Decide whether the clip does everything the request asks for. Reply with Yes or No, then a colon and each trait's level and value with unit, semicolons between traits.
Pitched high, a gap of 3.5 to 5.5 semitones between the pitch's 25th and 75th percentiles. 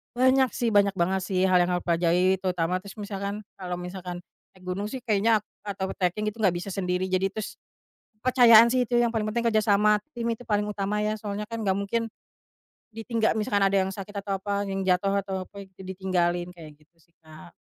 No: high, 200 Hz; average, 2.9 semitones